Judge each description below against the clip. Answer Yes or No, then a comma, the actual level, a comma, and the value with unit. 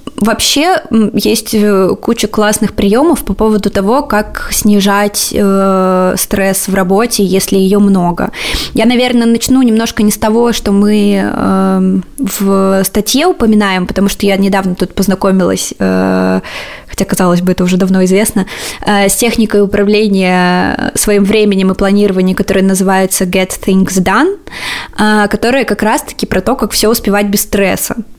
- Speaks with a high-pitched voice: Yes, high, 205 Hz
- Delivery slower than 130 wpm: No, average, 145 wpm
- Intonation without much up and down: Yes, narrow, 2.3 semitones